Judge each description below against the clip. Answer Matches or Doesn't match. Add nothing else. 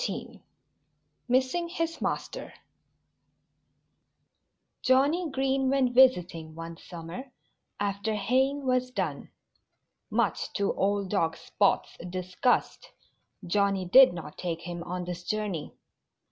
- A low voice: Doesn't match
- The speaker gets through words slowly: Matches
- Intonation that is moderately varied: Doesn't match